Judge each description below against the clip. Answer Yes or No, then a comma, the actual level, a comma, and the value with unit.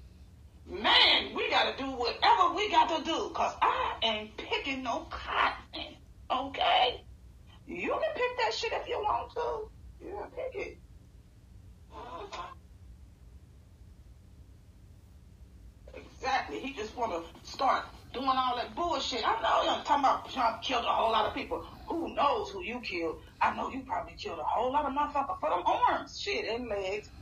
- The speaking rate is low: No, average, 155 wpm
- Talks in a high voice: Yes, high, 245 Hz